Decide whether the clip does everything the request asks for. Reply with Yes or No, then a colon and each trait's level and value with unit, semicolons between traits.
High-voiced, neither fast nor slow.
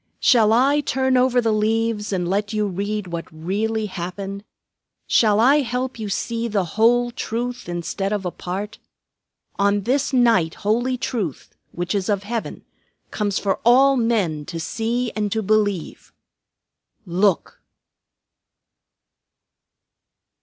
No: high, 215 Hz; slow, 130 wpm